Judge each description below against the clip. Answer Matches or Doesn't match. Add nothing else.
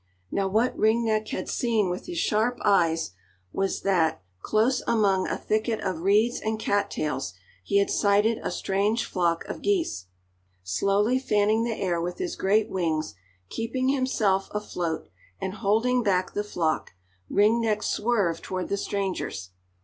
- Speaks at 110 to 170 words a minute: Matches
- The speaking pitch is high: Matches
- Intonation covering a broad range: Doesn't match